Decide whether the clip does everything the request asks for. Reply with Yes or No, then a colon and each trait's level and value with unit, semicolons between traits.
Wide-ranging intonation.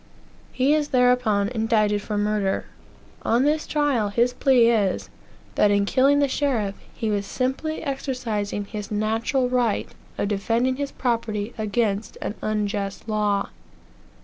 No: average, 3.7 semitones